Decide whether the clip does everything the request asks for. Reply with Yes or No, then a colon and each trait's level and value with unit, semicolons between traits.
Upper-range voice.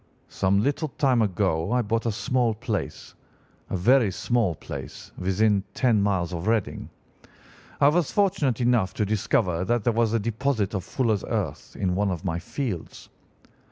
No: low, 110 Hz